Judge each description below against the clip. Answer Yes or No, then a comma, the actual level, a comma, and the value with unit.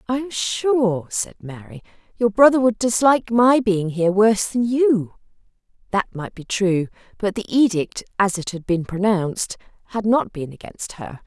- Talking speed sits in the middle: Yes, average, 170 wpm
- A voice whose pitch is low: No, high, 210 Hz